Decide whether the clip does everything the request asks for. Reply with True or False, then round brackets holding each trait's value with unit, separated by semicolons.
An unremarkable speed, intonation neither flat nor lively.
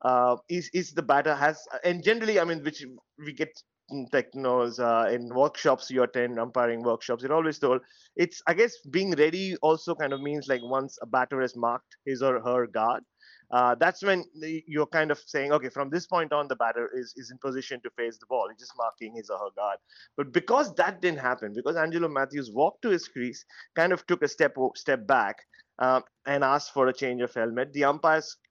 False (215 wpm; 4.4 semitones)